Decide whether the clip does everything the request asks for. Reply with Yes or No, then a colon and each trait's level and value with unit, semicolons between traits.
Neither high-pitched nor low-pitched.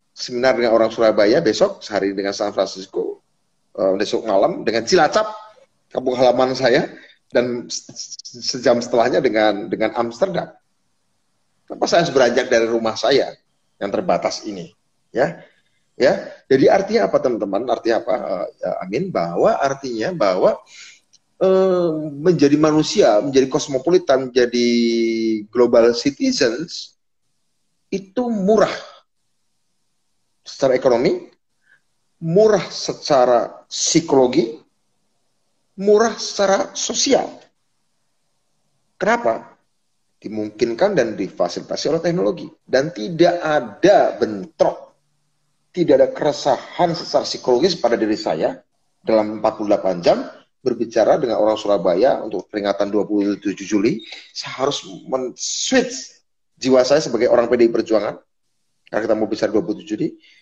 No: low, 130 Hz